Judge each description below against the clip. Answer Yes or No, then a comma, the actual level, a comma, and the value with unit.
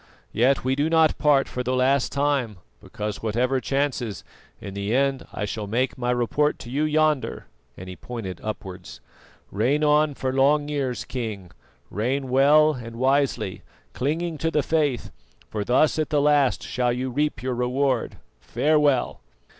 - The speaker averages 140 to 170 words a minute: Yes, average, 160 wpm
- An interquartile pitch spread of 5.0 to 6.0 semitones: No, average, 3.6 semitones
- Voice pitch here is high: No, low, 130 Hz